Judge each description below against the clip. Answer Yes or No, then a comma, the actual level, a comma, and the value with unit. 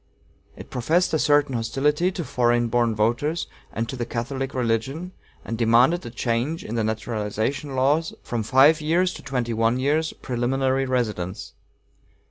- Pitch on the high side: No, low, 130 Hz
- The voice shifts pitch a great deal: No, average, 4.1 semitones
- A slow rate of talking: No, average, 160 wpm